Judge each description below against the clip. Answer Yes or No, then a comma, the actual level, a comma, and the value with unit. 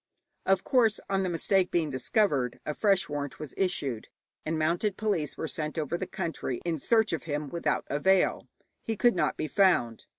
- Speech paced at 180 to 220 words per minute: Yes, average, 185 wpm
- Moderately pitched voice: Yes, medium, 170 Hz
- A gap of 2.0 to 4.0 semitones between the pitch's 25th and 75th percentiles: No, average, 4.5 semitones